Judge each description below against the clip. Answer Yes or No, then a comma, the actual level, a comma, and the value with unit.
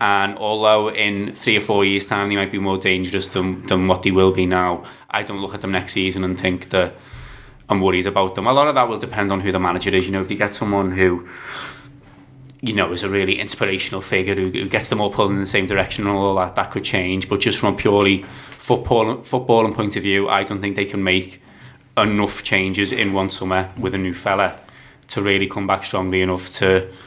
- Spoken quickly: Yes, fast, 235 wpm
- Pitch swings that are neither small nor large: No, narrow, 1.4 semitones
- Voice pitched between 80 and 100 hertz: Yes, very low, 95 Hz